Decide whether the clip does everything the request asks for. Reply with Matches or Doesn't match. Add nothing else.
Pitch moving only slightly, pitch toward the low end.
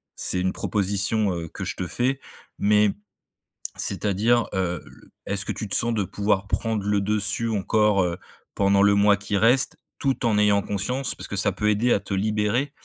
Matches